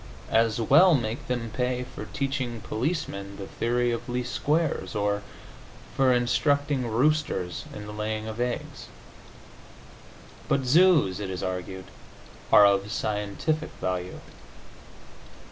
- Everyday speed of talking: No, slow, 120 wpm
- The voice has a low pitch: Yes, low, 120 Hz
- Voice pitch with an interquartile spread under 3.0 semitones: No, average, 4.7 semitones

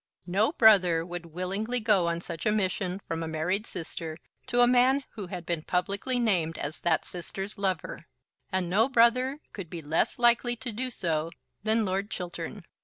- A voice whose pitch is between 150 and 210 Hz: Yes, high, 190 Hz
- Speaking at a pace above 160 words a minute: Yes, average, 180 wpm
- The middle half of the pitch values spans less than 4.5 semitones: No, average, 4.9 semitones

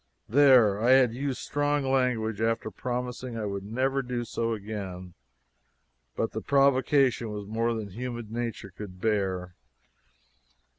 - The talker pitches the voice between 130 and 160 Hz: No, low, 115 Hz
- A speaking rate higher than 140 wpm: No, slow, 135 wpm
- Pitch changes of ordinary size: Yes, average, 3.5 semitones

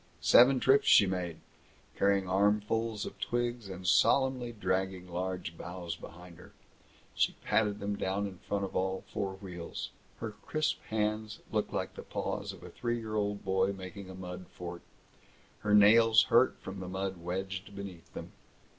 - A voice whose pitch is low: Yes, low, 100 Hz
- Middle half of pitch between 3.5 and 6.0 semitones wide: No, narrow, 2.6 semitones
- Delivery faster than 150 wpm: Yes, average, 165 wpm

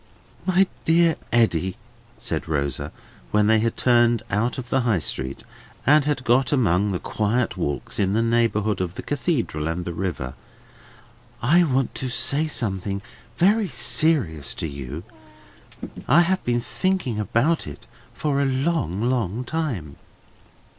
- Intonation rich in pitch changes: Yes, wide, 7.1 semitones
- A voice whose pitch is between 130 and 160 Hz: No, low, 115 Hz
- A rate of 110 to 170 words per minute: Yes, average, 145 wpm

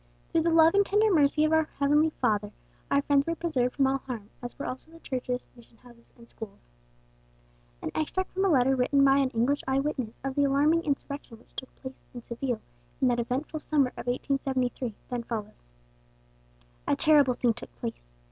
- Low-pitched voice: No, very high, 270 Hz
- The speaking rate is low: No, average, 195 wpm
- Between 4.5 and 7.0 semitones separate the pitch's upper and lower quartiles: No, average, 3.7 semitones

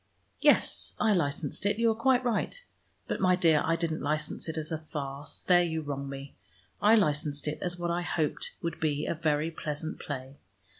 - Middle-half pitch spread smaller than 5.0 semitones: Yes, average, 3.2 semitones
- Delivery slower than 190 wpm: No, average, 195 wpm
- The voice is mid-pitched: Yes, medium, 160 Hz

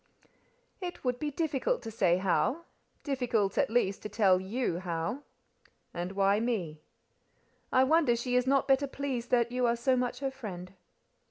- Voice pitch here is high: Yes, high, 240 Hz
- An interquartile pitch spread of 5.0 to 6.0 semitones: Yes, wide, 5.4 semitones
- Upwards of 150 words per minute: Yes, average, 160 wpm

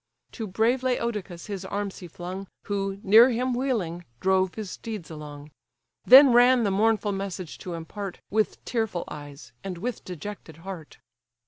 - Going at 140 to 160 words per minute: Yes, average, 150 wpm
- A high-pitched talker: Yes, high, 195 Hz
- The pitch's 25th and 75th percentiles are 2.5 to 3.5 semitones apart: No, average, 4.3 semitones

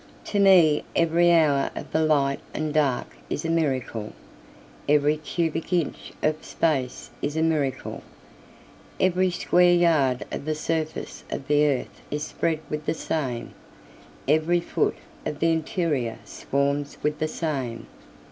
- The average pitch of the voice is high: No, medium, 155 Hz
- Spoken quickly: No, average, 140 wpm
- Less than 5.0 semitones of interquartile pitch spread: Yes, average, 2.7 semitones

